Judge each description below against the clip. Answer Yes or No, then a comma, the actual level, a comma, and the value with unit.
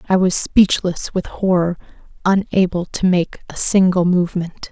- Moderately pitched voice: Yes, medium, 180 Hz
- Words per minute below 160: Yes, average, 140 wpm